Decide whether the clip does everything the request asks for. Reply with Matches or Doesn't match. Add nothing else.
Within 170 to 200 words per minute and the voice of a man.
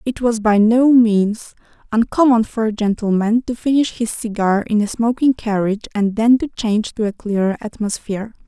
Doesn't match